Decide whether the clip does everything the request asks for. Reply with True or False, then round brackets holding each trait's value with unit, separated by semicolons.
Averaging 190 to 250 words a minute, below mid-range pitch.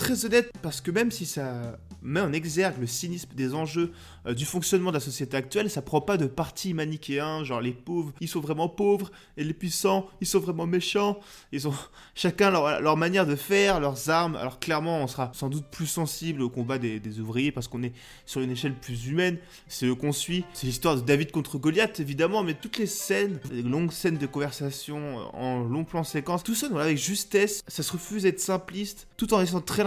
False (220 wpm; 160 Hz)